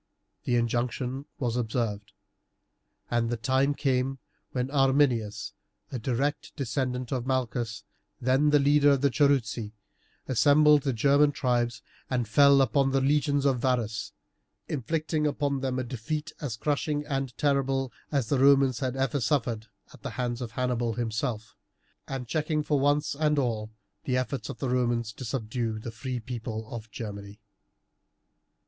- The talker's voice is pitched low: Yes, low, 130 Hz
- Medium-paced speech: Yes, average, 150 wpm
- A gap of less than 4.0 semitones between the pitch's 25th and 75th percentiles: Yes, average, 3.2 semitones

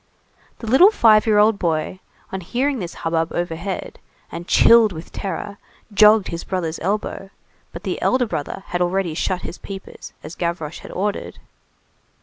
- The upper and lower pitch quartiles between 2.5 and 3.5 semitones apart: No, average, 3.9 semitones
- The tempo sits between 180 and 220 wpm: No, average, 155 wpm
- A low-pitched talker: No, high, 190 Hz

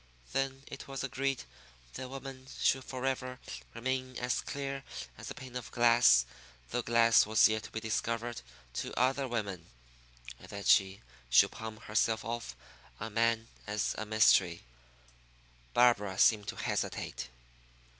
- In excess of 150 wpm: No, average, 140 wpm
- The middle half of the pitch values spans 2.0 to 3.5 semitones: Yes, average, 3.1 semitones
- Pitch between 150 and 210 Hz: No, low, 115 Hz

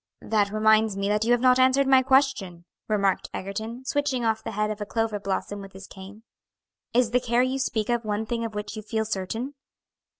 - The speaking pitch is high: Yes, high, 220 Hz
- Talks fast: Yes, fast, 210 wpm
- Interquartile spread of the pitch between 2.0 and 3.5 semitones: Yes, average, 3.2 semitones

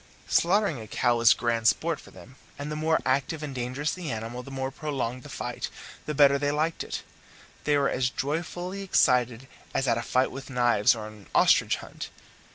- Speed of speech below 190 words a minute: No, average, 195 wpm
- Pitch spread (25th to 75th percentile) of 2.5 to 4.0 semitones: Yes, average, 3.7 semitones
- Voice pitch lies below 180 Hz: Yes, low, 135 Hz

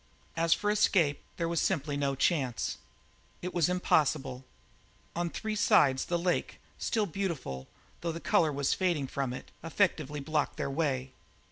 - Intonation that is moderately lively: Yes, average, 4.1 semitones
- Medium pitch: Yes, medium, 155 Hz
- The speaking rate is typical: Yes, average, 150 wpm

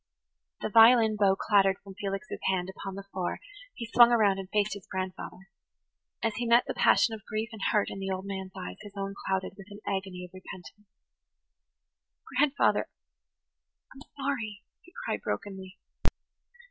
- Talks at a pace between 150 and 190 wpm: Yes, average, 160 wpm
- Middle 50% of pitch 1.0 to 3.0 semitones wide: Yes, average, 2.7 semitones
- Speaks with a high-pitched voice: Yes, high, 200 Hz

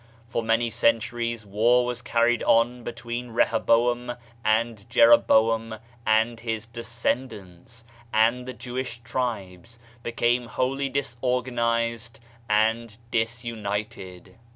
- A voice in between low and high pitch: No, low, 115 Hz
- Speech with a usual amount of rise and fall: No, narrow, 1.3 semitones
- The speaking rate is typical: No, slow, 100 wpm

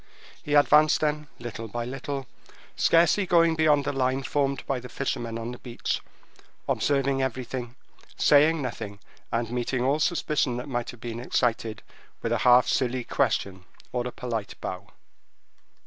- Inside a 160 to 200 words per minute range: No, average, 150 wpm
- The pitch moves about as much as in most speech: Yes, average, 3.3 semitones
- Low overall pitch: Yes, low, 130 Hz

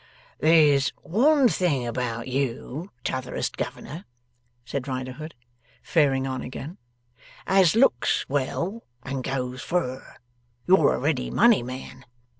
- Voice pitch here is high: No, medium, 140 Hz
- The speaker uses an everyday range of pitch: Yes, average, 4.9 semitones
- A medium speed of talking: No, slow, 110 wpm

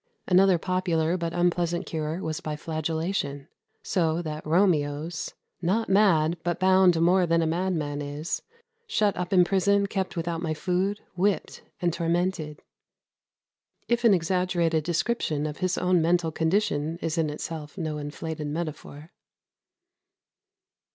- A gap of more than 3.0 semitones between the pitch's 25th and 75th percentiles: No, average, 2.7 semitones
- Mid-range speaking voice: Yes, medium, 170 Hz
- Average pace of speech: No, slow, 130 wpm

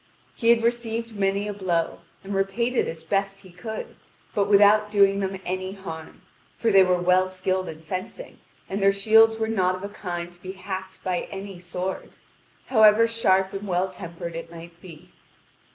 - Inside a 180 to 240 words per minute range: Yes, average, 185 wpm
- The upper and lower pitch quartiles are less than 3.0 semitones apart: Yes, narrow, 2.4 semitones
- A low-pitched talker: No, high, 195 Hz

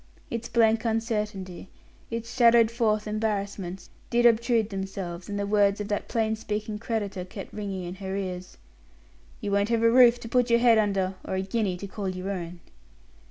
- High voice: Yes, high, 210 Hz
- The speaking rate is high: No, average, 180 wpm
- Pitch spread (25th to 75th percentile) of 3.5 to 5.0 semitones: No, average, 3.0 semitones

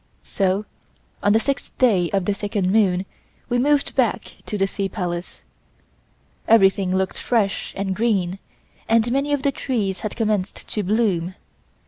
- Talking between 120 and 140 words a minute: No, average, 150 wpm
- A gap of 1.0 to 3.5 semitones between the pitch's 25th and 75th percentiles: Yes, average, 3.2 semitones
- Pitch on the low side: No, high, 205 Hz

